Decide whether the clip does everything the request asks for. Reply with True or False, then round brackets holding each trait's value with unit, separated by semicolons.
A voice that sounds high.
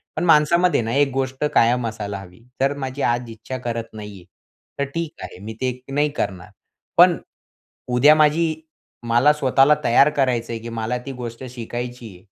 False (125 Hz)